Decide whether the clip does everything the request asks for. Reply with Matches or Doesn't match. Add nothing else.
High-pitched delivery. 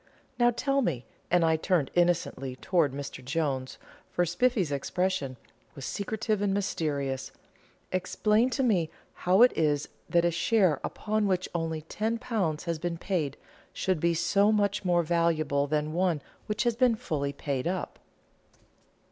Doesn't match